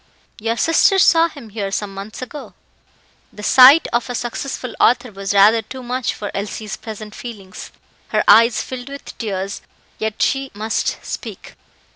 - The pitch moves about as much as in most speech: Yes, average, 3.7 semitones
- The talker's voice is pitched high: Yes, high, 230 Hz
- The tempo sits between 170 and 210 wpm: No, average, 160 wpm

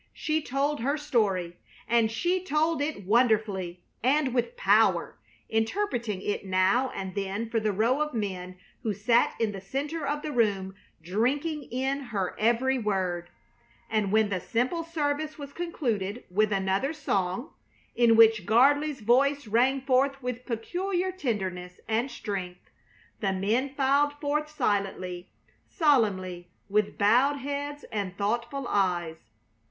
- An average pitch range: No, wide, 6.2 semitones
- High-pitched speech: Yes, high, 235 Hz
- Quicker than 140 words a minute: No, slow, 135 wpm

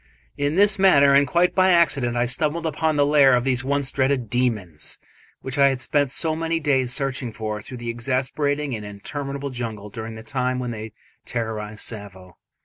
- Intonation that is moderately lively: Yes, average, 3.9 semitones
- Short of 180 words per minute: No, average, 185 wpm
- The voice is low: Yes, low, 130 Hz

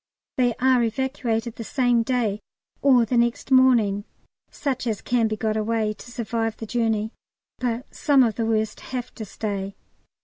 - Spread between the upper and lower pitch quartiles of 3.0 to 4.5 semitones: No, narrow, 2.4 semitones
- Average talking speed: Yes, average, 165 wpm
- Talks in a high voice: Yes, high, 230 Hz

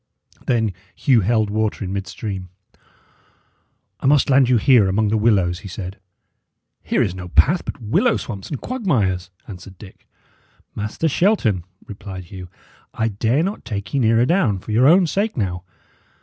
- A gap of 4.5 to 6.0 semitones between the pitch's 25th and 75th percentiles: Yes, wide, 5.6 semitones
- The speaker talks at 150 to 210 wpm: Yes, average, 160 wpm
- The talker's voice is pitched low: Yes, low, 110 Hz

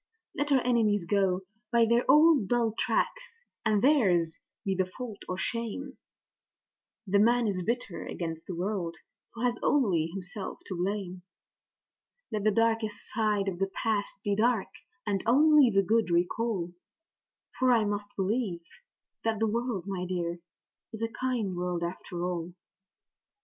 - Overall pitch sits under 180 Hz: No, high, 205 Hz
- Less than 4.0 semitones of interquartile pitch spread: No, average, 4.3 semitones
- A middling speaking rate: Yes, average, 150 wpm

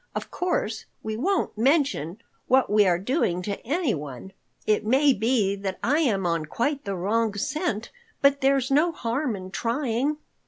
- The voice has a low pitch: No, high, 230 Hz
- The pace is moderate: Yes, average, 160 wpm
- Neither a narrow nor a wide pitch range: No, wide, 6.0 semitones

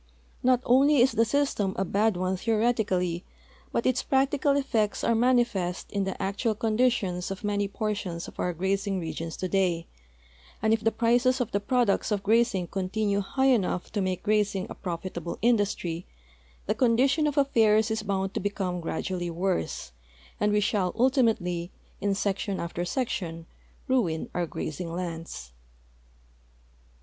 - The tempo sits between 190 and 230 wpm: No, average, 155 wpm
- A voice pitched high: Yes, high, 205 Hz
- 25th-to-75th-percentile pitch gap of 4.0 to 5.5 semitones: Yes, average, 4.4 semitones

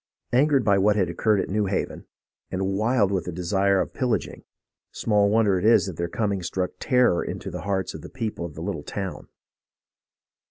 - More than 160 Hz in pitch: No, low, 100 Hz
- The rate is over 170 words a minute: Yes, average, 195 wpm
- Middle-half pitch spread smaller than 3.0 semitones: Yes, narrow, 2.6 semitones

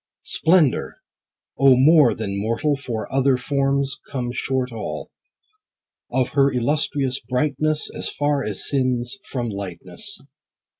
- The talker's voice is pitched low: Yes, low, 130 Hz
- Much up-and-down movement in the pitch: No, average, 2.7 semitones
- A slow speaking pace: Yes, slow, 115 wpm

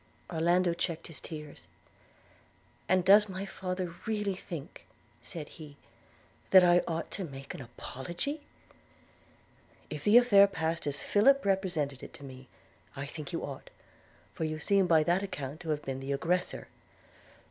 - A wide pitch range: No, average, 4.6 semitones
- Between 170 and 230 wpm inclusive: No, average, 150 wpm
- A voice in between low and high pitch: Yes, medium, 170 Hz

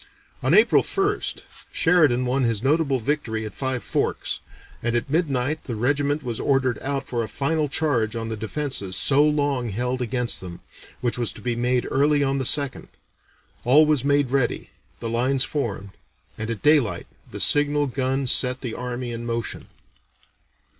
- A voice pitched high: No, low, 130 Hz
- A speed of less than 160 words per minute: No, average, 165 wpm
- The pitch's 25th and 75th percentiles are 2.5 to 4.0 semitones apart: Yes, average, 3.5 semitones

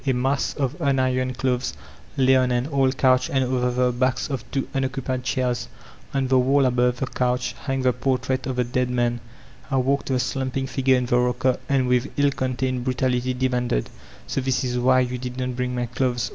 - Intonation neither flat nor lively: No, narrow, 1.1 semitones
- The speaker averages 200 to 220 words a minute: Yes, fast, 205 wpm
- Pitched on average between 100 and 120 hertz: No, low, 130 Hz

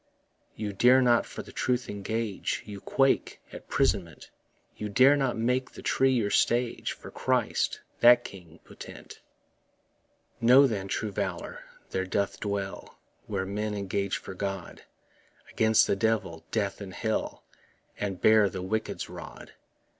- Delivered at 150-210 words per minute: No, average, 140 wpm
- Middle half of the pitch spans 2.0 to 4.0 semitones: Yes, average, 3.3 semitones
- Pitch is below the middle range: Yes, low, 105 Hz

